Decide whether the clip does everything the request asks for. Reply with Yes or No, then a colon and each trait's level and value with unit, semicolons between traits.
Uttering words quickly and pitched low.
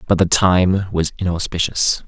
No: average, 145 wpm; very low, 90 Hz